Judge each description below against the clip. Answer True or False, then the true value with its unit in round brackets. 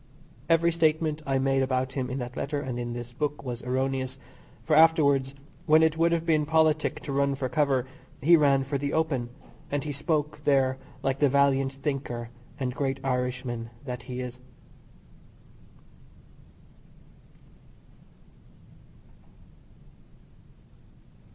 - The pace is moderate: False (130 wpm)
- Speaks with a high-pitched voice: False (135 Hz)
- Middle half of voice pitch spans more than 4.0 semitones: False (2.8 semitones)